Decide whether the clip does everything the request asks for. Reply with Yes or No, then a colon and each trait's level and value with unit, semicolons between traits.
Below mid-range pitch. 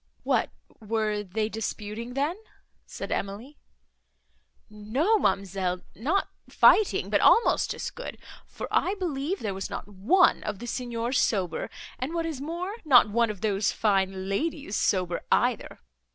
No: high, 225 Hz